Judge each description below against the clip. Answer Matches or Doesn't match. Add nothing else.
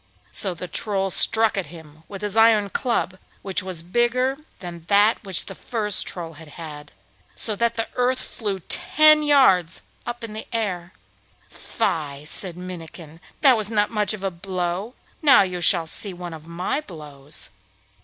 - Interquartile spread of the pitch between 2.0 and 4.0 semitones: Doesn't match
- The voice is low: Doesn't match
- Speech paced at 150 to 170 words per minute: Matches